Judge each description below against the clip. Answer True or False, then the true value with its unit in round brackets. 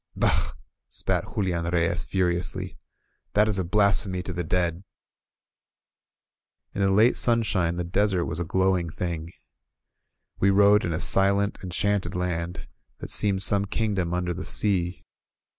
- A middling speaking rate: True (145 wpm)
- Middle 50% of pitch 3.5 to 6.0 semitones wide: False (2.5 semitones)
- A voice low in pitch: True (95 Hz)